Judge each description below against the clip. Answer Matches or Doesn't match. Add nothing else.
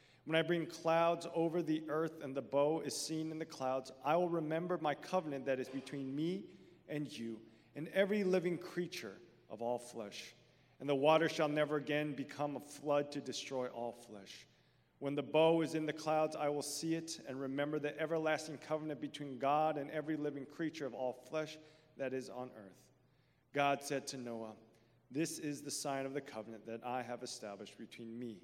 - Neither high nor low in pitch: Matches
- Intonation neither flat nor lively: Matches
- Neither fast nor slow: Matches